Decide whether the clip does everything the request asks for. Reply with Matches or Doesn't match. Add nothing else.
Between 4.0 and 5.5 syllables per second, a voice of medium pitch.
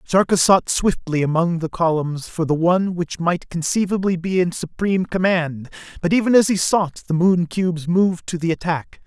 Matches